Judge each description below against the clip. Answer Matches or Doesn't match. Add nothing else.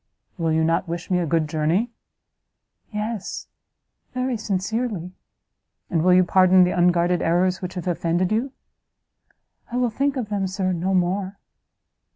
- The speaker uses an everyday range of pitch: Matches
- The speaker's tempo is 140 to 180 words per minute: Matches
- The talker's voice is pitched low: Doesn't match